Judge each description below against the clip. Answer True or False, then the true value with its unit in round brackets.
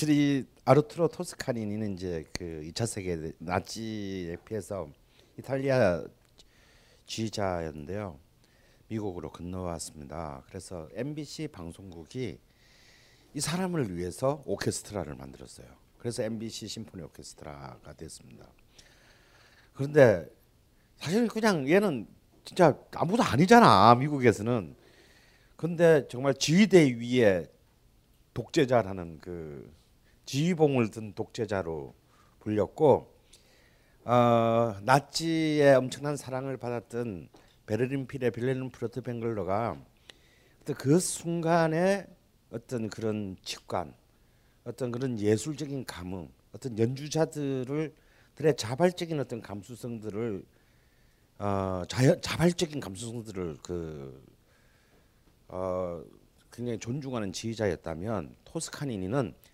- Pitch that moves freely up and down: True (6.7 semitones)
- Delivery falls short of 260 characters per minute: True (245 characters per minute)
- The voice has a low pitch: True (115 Hz)